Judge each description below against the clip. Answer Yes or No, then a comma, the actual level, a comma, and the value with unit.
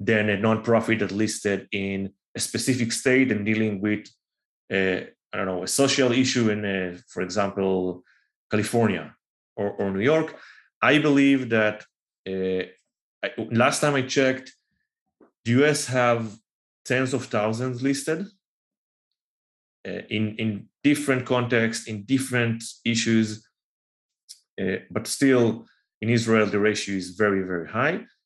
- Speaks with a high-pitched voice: No, low, 110 Hz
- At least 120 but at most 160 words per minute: Yes, slow, 135 wpm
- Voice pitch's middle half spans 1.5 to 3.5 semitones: No, average, 4.1 semitones